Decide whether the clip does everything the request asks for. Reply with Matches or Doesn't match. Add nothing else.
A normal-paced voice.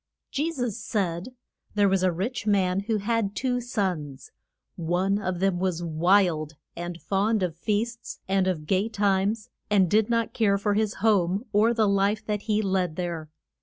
Matches